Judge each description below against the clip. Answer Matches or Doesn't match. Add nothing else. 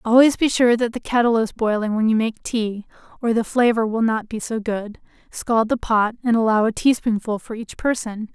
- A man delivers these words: Doesn't match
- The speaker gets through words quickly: Matches